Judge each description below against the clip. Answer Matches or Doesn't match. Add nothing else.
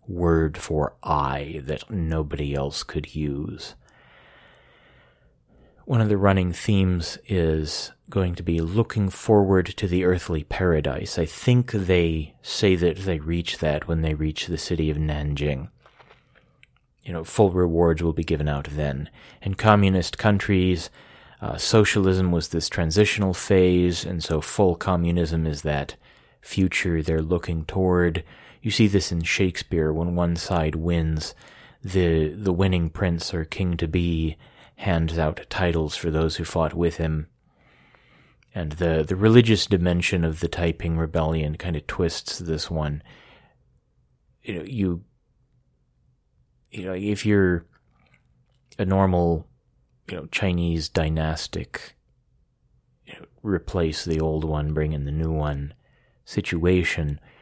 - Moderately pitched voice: Doesn't match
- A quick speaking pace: Doesn't match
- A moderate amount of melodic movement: Matches